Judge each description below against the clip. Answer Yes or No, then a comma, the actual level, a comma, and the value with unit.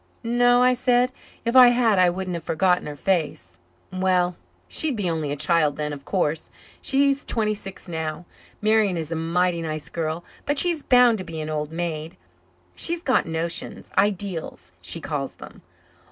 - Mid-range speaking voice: Yes, medium, 180 Hz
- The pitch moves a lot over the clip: Yes, wide, 6.4 semitones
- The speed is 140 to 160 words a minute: No, average, 170 wpm